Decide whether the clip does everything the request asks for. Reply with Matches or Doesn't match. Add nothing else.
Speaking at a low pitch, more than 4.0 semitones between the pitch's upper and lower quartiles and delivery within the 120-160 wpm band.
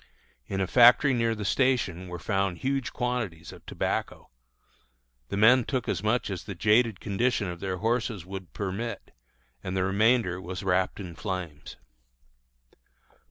Matches